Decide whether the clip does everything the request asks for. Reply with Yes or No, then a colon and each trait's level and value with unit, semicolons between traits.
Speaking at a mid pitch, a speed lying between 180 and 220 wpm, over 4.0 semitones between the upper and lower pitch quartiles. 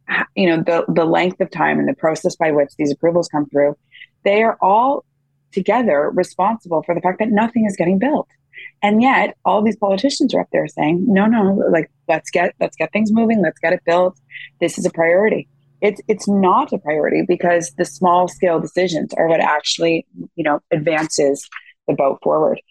Yes: medium, 175 Hz; average, 195 wpm; average, 4.4 semitones